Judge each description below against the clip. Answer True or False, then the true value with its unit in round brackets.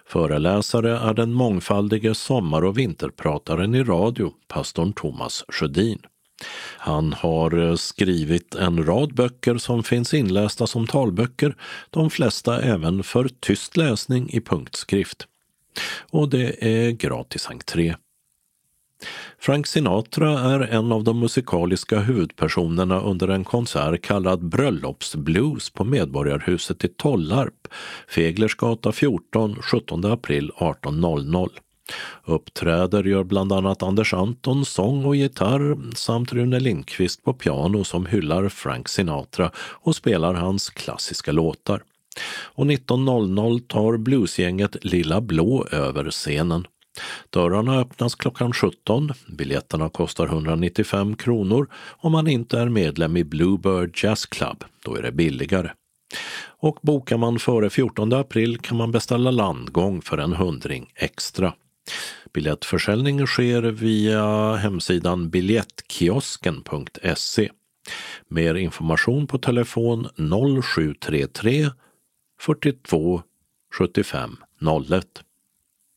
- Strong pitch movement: True (5.7 semitones)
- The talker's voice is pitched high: False (110 Hz)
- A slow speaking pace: True (110 wpm)